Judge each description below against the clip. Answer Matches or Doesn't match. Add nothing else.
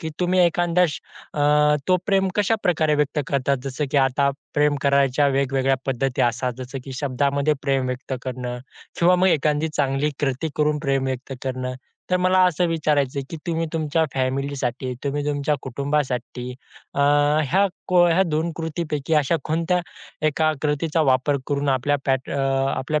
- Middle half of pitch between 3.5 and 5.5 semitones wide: Doesn't match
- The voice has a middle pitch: Matches